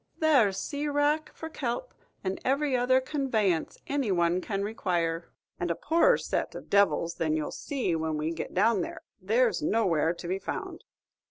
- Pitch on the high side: Yes, high, 205 Hz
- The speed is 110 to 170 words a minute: No, average, 180 wpm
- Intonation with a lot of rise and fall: Yes, wide, 8.0 semitones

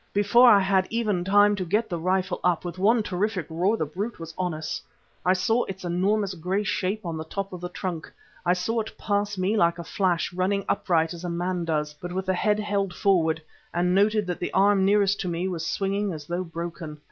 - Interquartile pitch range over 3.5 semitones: No, average, 2.8 semitones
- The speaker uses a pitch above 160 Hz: Yes, medium, 185 Hz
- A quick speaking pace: Yes, fast, 225 wpm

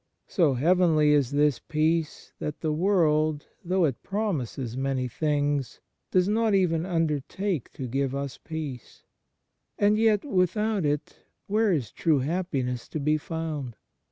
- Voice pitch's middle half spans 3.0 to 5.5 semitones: Yes, average, 4.6 semitones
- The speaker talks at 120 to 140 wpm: Yes, slow, 135 wpm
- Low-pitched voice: No, medium, 155 Hz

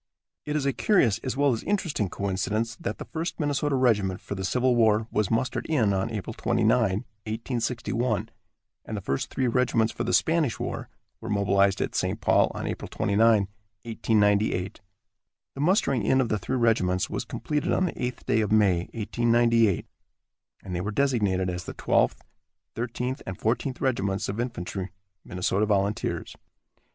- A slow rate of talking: No, average, 165 wpm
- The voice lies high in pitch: No, low, 110 Hz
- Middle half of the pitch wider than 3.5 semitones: Yes, average, 3.9 semitones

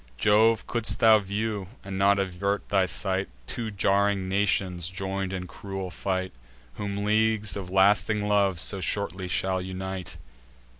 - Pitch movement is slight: Yes, narrow, 1.6 semitones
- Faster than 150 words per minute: No, average, 140 wpm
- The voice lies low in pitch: Yes, low, 100 Hz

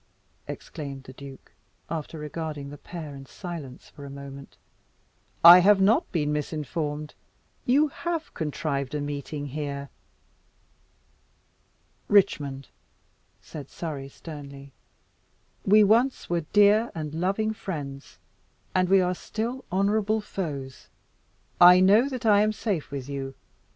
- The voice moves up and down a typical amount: No, wide, 6.1 semitones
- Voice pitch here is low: No, medium, 160 Hz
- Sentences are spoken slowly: Yes, slow, 120 wpm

